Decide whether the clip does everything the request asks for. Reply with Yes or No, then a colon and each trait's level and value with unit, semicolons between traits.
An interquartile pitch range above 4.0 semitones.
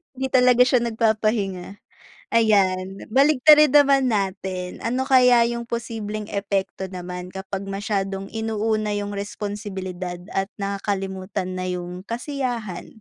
No: average, 3.6 semitones